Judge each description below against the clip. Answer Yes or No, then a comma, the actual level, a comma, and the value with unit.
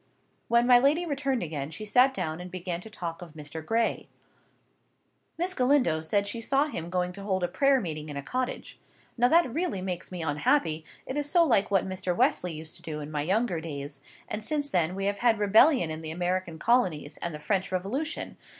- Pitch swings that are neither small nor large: No, wide, 7.4 semitones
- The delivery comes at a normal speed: No, fast, 210 wpm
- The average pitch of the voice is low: No, high, 190 Hz